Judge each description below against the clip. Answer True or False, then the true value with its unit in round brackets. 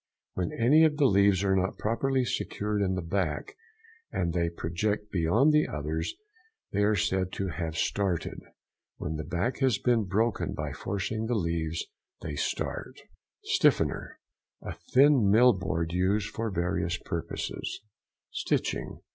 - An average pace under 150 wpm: True (140 wpm)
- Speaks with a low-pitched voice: True (95 Hz)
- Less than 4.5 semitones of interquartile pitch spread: False (4.8 semitones)